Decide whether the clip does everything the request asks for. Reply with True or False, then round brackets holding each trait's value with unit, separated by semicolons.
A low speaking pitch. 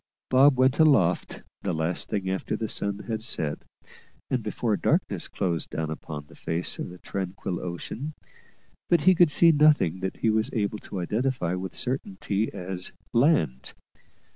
True (100 Hz)